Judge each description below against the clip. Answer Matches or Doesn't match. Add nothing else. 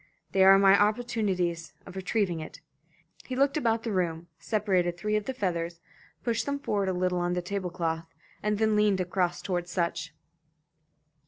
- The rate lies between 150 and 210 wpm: Matches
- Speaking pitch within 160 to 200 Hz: Matches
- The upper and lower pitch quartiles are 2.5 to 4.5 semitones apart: Matches